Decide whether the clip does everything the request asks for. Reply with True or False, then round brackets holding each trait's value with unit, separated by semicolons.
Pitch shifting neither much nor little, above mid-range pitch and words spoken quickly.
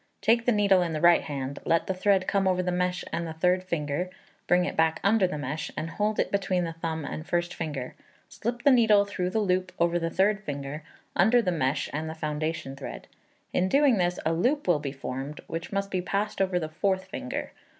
False (3.8 semitones; 180 Hz; 220 wpm)